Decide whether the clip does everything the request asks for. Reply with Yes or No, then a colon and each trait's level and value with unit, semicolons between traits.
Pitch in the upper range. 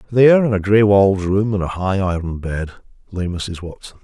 No: low, 100 Hz